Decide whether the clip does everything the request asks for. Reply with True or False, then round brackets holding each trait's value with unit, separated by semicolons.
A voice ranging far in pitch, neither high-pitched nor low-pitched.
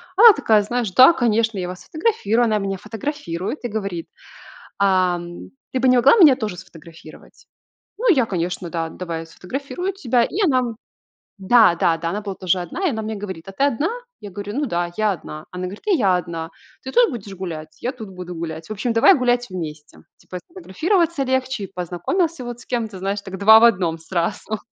False (5.8 semitones; 205 Hz)